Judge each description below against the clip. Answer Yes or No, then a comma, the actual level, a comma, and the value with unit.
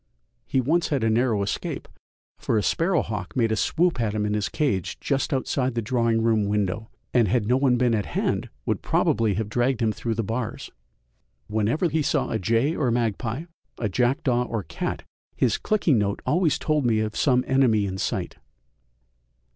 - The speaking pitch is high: No, low, 115 Hz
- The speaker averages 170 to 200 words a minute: Yes, average, 185 wpm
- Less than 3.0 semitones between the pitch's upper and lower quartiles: No, average, 3.6 semitones